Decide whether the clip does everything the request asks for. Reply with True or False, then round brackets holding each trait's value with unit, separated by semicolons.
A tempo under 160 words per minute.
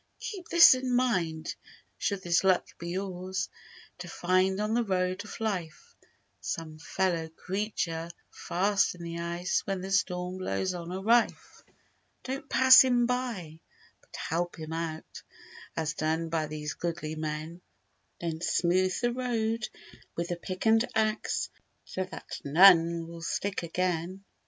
True (145 wpm)